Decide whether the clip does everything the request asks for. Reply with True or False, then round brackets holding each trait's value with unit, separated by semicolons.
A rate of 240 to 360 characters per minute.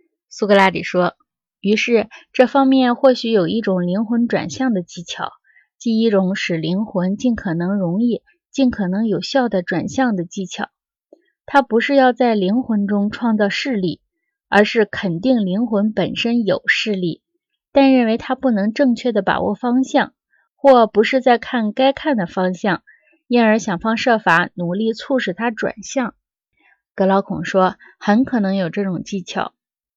False (230 characters per minute)